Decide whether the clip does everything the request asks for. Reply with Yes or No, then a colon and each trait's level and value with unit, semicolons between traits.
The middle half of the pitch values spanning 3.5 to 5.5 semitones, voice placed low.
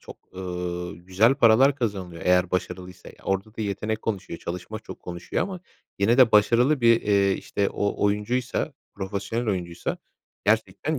Yes: average, 4.0 semitones; low, 100 Hz